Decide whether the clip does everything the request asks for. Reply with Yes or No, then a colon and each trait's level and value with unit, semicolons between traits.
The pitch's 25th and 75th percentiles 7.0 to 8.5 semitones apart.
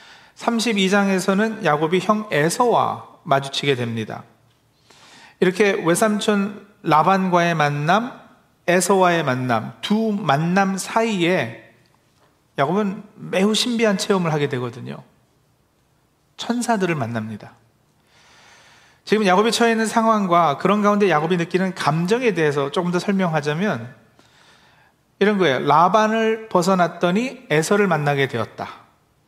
No: wide, 6.4 semitones